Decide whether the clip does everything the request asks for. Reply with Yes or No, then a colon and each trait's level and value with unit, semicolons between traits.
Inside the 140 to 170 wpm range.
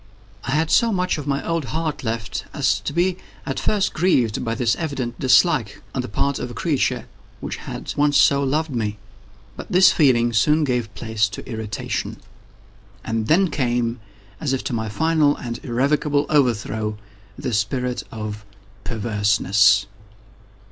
Yes: average, 155 wpm